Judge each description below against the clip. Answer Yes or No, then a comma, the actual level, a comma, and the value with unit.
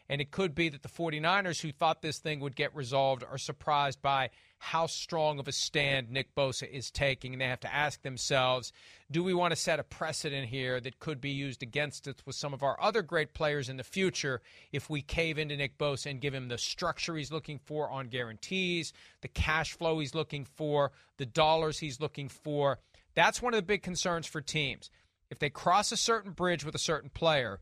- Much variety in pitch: No, average, 3.1 semitones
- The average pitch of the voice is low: No, medium, 145 Hz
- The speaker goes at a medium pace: No, fast, 220 wpm